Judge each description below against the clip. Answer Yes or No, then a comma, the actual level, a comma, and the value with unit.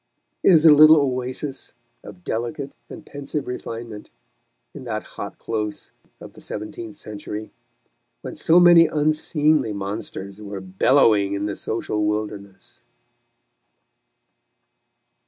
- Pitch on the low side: Yes, low, 115 Hz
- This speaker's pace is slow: Yes, slow, 115 wpm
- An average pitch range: No, wide, 6.1 semitones